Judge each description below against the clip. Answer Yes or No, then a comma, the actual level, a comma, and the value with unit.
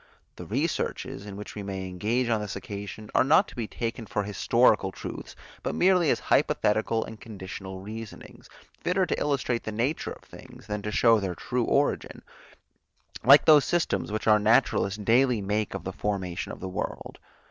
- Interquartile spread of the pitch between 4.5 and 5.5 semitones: No, average, 3.6 semitones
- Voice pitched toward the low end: Yes, low, 110 Hz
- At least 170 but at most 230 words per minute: Yes, average, 180 wpm